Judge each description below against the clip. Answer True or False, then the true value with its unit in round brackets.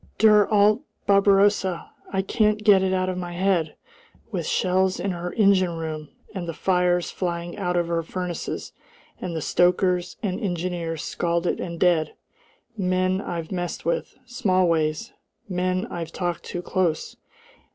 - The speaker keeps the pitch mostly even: True (2.0 semitones)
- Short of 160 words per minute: True (145 wpm)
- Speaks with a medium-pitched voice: True (180 Hz)